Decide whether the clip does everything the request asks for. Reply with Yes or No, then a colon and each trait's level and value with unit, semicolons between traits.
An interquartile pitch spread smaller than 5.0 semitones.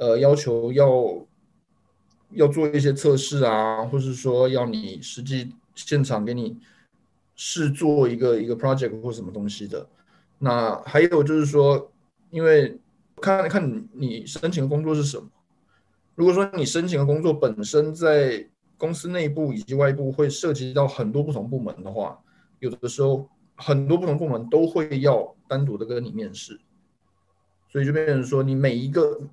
Yes: average, 4.0 semitones